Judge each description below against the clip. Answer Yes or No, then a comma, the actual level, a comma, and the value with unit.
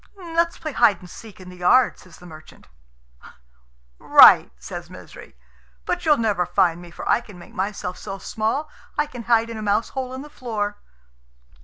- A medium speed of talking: Yes, average, 185 wpm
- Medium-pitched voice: No, high, 215 Hz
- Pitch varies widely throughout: Yes, wide, 5.9 semitones